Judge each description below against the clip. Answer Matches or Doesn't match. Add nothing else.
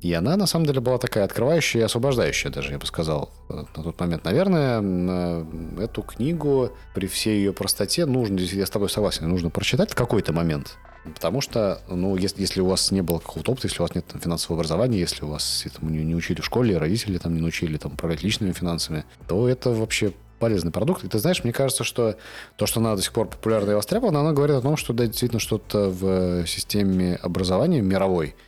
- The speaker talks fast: Matches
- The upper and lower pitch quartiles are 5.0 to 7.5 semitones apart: Matches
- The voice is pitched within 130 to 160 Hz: Doesn't match